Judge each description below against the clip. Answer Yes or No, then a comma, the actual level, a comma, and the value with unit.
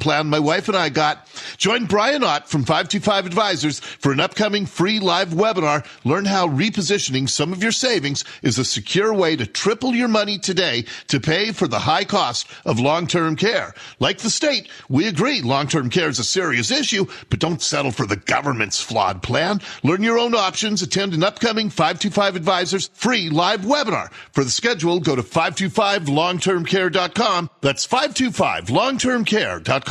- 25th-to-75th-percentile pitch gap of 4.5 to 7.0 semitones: Yes, wide, 5.4 semitones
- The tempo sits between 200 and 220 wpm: No, average, 170 wpm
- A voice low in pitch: No, high, 190 Hz